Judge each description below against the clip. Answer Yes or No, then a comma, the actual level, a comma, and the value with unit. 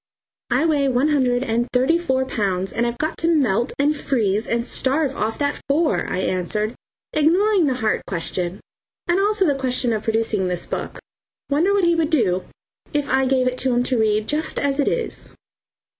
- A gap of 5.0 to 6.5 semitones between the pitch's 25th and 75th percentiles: Yes, average, 5.3 semitones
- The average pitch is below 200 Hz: No, very high, 260 Hz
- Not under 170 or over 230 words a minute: Yes, average, 190 wpm